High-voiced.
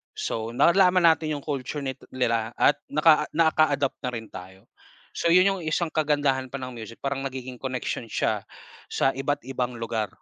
No: low, 135 Hz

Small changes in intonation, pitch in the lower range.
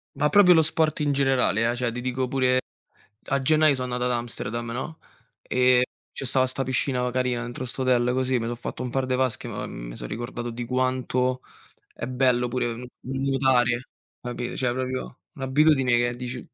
Yes: narrow, 1.5 semitones; low, 125 Hz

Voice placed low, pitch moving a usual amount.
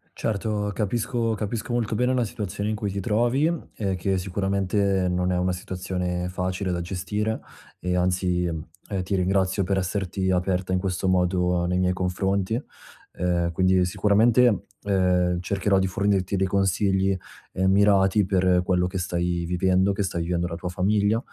No: very low, 95 Hz; narrow, 2.0 semitones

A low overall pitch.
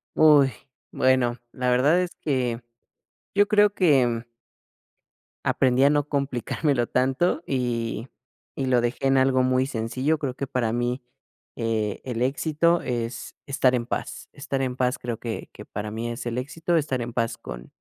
Yes: low, 130 Hz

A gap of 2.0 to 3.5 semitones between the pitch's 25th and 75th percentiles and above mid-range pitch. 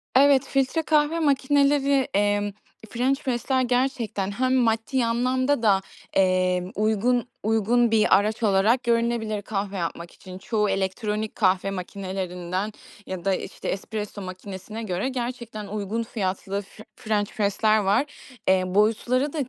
No: average, 4.3 semitones; high, 215 Hz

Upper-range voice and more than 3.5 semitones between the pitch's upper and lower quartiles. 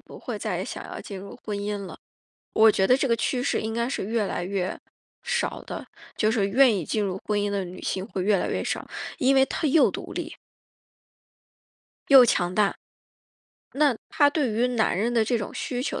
Yes: high, 220 Hz; average, 4.1 semitones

